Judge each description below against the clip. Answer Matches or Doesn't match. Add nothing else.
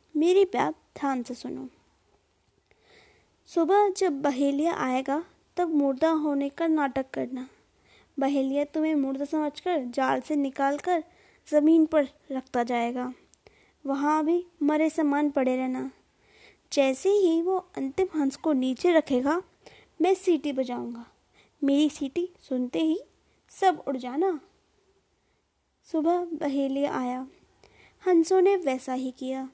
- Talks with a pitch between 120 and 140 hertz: Doesn't match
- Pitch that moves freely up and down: Doesn't match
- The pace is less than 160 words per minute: Matches